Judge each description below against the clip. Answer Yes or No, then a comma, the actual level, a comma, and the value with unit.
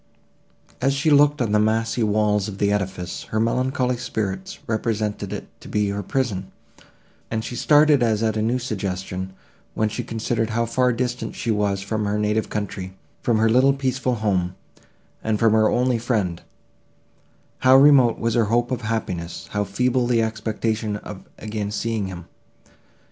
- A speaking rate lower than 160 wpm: No, average, 165 wpm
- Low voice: Yes, low, 110 Hz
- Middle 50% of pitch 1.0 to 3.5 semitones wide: Yes, average, 3.0 semitones